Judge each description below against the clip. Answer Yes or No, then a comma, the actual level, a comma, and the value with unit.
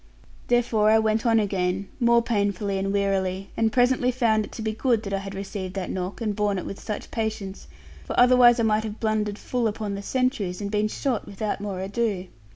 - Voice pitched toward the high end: Yes, high, 210 Hz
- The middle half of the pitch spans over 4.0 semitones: No, narrow, 2.5 semitones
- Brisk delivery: Yes, fast, 210 wpm